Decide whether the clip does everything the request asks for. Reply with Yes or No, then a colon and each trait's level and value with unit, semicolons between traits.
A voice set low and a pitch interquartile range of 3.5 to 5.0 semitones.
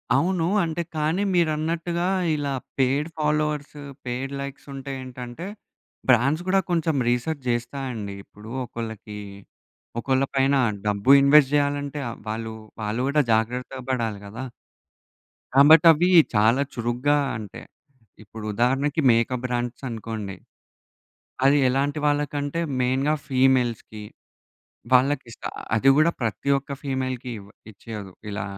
Yes: low, 130 Hz; average, 3.9 semitones